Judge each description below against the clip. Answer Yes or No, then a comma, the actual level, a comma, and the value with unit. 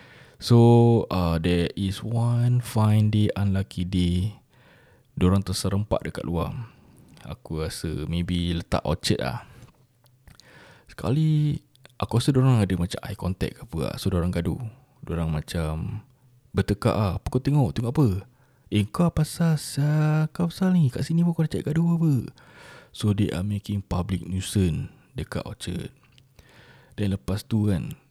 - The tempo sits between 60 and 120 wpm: No, average, 145 wpm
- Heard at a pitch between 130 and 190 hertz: No, low, 110 Hz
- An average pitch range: No, wide, 6.2 semitones